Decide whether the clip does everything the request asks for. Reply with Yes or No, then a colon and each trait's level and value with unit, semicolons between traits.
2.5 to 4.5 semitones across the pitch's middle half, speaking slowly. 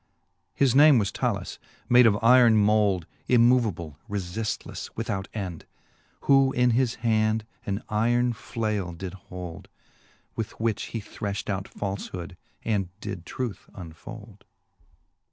Yes: average, 3.4 semitones; slow, 120 wpm